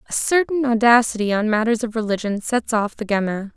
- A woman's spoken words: Yes, female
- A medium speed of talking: Yes, average, 185 wpm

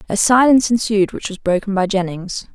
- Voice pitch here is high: Yes, high, 205 Hz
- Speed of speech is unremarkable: Yes, average, 190 wpm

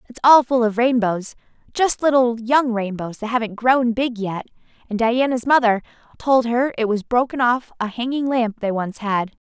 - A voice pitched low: No, high, 235 Hz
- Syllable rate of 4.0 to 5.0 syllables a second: Yes, 4.7 syllables/s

